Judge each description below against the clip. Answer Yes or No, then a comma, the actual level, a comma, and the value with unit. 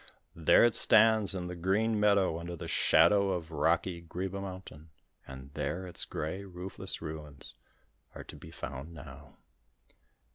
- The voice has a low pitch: Yes, very low, 90 Hz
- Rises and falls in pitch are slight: No, average, 3.5 semitones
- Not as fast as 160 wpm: Yes, average, 145 wpm